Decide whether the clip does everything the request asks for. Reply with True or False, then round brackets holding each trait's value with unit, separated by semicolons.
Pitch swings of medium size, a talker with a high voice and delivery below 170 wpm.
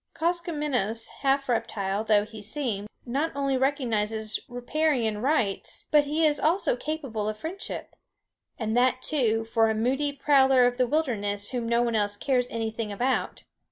True (4.5 semitones; 245 Hz; 155 wpm)